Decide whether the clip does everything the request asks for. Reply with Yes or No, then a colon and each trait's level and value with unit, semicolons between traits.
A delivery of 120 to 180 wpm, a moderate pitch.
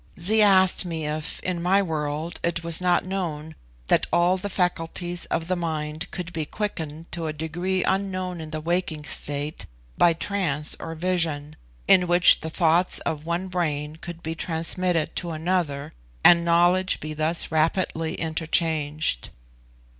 Yes: average, 155 wpm; medium, 170 Hz